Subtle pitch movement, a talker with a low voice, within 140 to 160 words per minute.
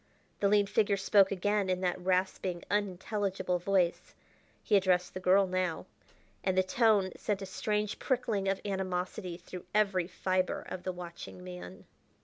No: narrow, 1.8 semitones; medium, 185 Hz; average, 150 wpm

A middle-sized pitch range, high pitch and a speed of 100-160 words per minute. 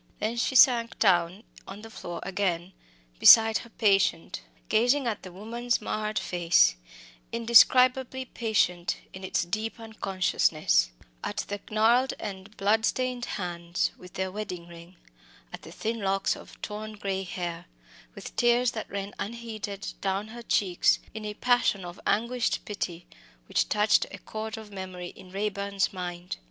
Yes: average, 3.4 semitones; high, 205 Hz; average, 145 wpm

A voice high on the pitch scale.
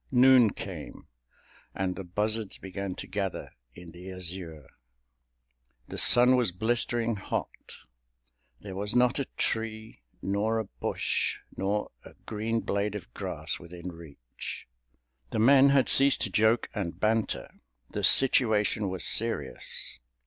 No: low, 105 Hz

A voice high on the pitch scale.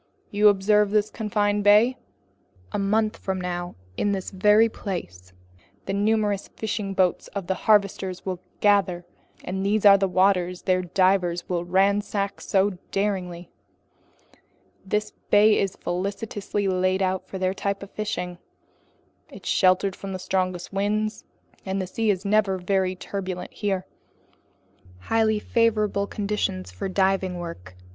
Yes: high, 195 Hz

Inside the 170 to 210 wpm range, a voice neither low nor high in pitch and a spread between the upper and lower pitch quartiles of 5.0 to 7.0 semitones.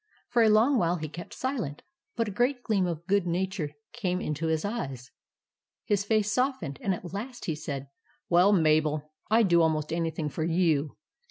Yes: average, 190 wpm; medium, 175 Hz; wide, 5.5 semitones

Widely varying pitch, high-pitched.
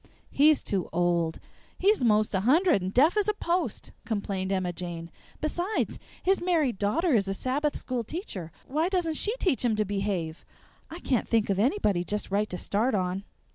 Yes: wide, 8.9 semitones; high, 220 Hz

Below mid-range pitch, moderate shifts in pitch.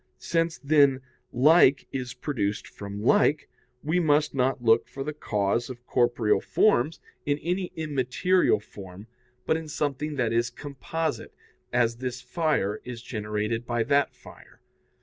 Yes: low, 130 Hz; average, 4.5 semitones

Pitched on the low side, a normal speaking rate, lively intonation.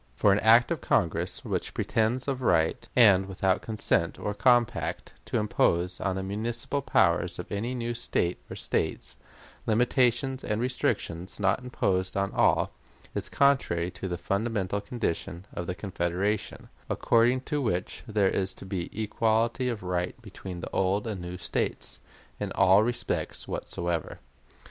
No: low, 100 Hz; average, 150 wpm; average, 4.2 semitones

